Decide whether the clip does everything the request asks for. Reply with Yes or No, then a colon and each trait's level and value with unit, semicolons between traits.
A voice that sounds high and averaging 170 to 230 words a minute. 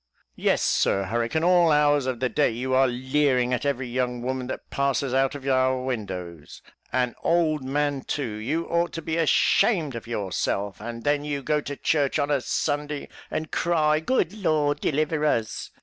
No: medium, 140 Hz; average, 180 wpm